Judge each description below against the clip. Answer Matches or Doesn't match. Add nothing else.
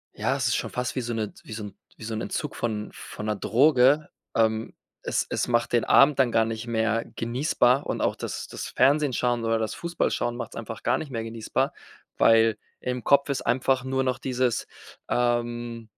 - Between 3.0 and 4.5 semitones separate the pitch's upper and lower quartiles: Doesn't match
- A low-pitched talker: Matches